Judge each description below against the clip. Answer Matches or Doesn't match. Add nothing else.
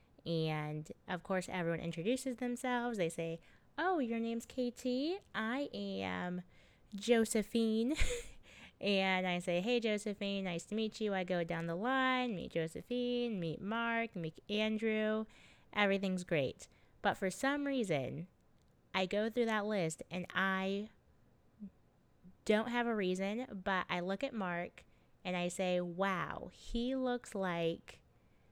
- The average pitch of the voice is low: Doesn't match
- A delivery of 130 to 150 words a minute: Matches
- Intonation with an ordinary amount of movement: Matches